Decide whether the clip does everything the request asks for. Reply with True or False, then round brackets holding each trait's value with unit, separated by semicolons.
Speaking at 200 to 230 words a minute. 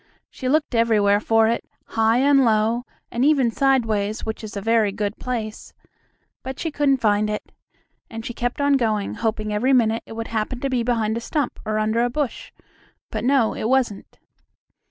False (185 wpm)